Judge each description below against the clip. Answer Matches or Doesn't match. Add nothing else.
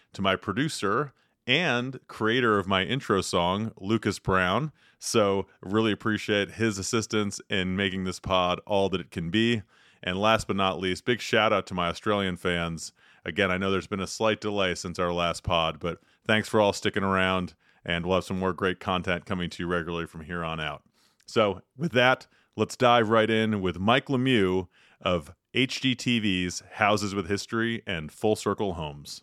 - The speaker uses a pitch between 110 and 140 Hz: Doesn't match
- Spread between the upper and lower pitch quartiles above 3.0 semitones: Matches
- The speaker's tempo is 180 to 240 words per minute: Matches